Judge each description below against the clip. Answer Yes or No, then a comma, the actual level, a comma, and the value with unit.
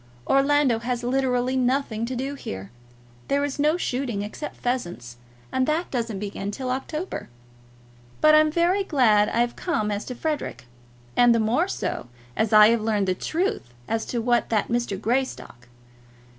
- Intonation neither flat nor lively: Yes, average, 4.6 semitones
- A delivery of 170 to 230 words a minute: No, average, 155 wpm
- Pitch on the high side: Yes, high, 245 Hz